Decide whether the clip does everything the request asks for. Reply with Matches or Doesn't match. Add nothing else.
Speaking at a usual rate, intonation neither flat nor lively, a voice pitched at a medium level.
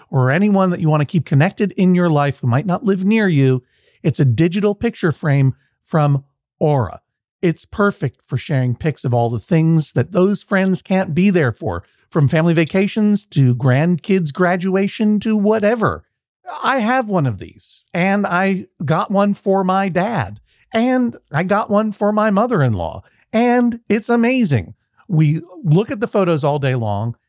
Doesn't match